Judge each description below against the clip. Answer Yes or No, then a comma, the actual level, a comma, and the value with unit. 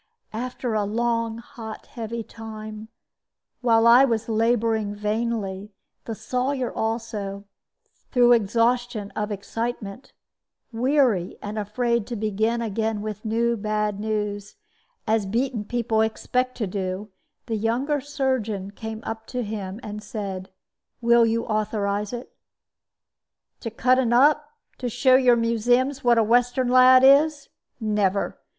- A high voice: Yes, high, 225 Hz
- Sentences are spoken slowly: Yes, slow, 130 wpm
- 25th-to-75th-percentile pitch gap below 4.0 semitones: Yes, narrow, 2.4 semitones